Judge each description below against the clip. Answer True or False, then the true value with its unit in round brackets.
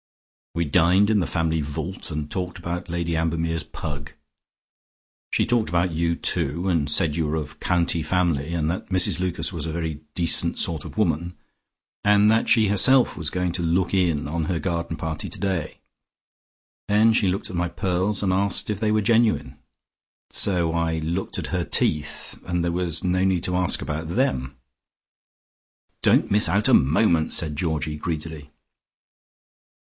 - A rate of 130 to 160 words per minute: False (170 wpm)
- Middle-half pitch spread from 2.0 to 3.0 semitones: True (2.7 semitones)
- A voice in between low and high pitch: False (85 Hz)